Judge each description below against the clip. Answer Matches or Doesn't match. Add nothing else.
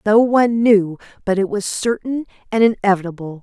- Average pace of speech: Matches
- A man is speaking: Doesn't match